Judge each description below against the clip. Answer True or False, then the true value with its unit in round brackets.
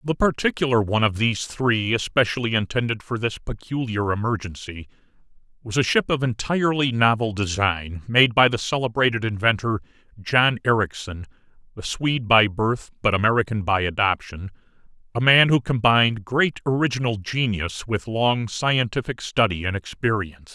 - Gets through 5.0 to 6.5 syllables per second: True (5.2 syllables/s)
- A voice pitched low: True (115 Hz)